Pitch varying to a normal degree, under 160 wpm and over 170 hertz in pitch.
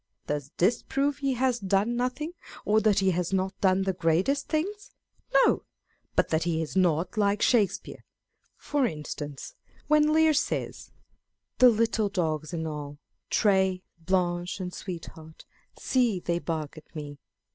No: wide, 6.6 semitones; average, 150 wpm; high, 190 Hz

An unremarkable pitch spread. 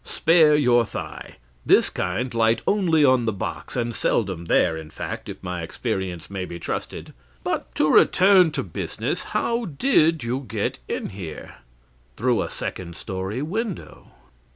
No: wide, 8.9 semitones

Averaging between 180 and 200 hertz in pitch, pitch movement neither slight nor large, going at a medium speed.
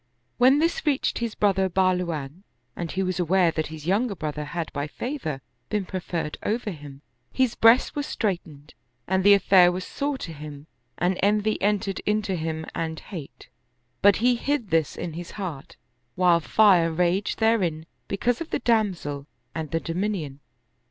Yes: medium, 185 Hz; average, 4.8 semitones; average, 165 wpm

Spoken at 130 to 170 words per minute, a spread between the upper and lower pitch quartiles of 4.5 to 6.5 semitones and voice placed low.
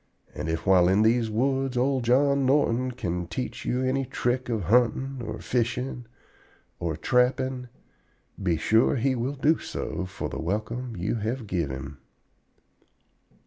Yes: average, 155 wpm; average, 5.2 semitones; low, 120 Hz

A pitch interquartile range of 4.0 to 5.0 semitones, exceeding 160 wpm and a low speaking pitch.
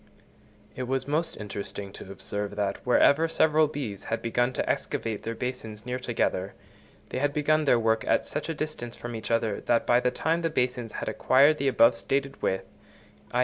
Yes: average, 4.4 semitones; average, 190 wpm; low, 125 Hz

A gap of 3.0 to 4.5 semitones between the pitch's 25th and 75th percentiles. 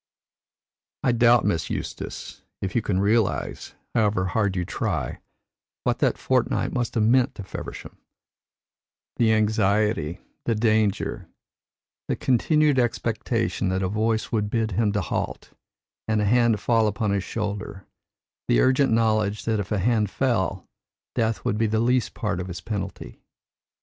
No: narrow, 2.4 semitones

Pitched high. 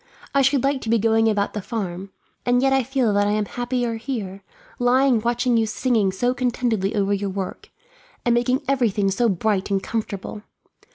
Yes: high, 225 Hz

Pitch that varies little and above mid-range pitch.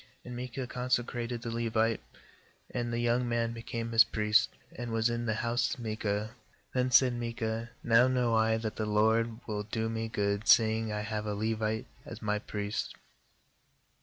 No: narrow, 1.4 semitones; low, 115 Hz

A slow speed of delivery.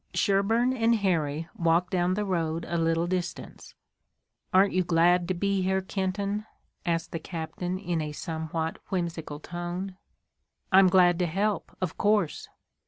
No: average, 145 wpm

